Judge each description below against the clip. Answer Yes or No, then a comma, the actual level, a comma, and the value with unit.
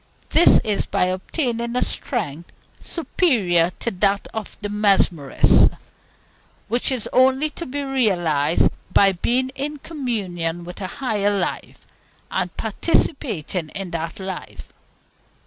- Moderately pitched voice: No, high, 205 Hz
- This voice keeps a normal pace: No, slow, 120 wpm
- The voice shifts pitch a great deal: Yes, wide, 6.4 semitones